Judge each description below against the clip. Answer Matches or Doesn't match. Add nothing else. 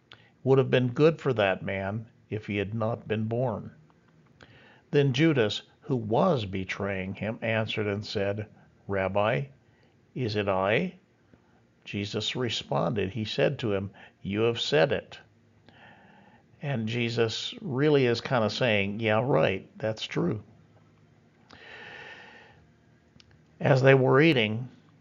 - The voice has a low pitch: Matches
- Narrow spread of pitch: Doesn't match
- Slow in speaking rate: Matches